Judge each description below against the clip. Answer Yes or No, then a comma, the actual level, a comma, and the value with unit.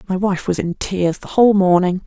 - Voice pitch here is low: No, high, 190 Hz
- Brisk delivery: Yes, fast, 235 wpm